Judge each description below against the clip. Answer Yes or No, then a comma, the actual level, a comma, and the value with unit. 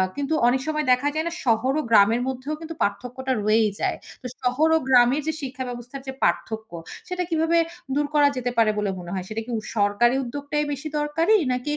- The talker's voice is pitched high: Yes, very high, 255 Hz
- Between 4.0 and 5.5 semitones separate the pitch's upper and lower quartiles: Yes, average, 4.6 semitones